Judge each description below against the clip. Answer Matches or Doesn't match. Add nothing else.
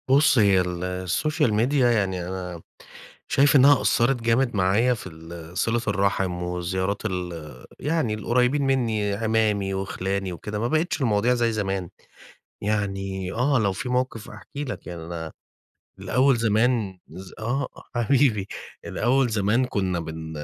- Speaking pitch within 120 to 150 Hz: Doesn't match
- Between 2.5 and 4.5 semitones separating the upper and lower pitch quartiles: Doesn't match